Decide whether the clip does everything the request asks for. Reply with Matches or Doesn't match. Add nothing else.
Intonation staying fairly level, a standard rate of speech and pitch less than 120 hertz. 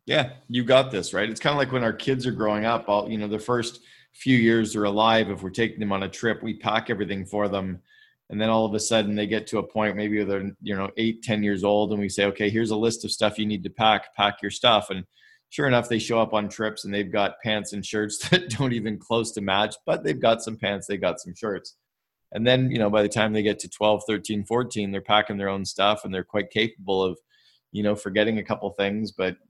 Doesn't match